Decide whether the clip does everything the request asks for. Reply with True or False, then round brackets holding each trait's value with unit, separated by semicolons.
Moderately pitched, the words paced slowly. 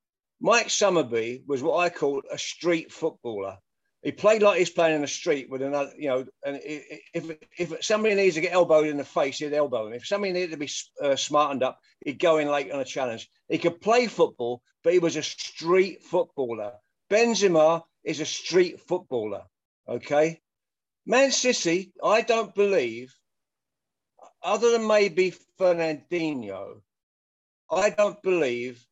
False (165 Hz; 160 wpm)